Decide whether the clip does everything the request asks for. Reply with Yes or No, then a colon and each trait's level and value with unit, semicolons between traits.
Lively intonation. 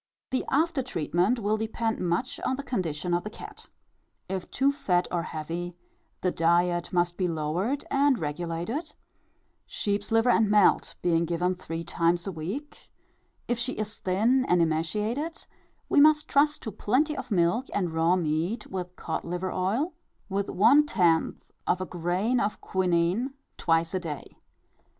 Yes: wide, 5.8 semitones